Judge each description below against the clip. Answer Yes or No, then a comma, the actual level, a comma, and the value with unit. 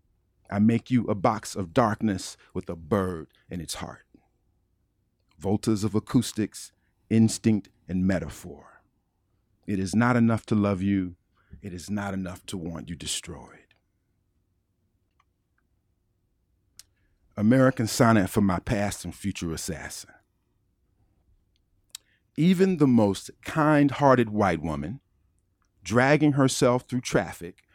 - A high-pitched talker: No, low, 100 Hz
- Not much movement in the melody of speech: No, average, 3.4 semitones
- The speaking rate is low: Yes, slow, 115 wpm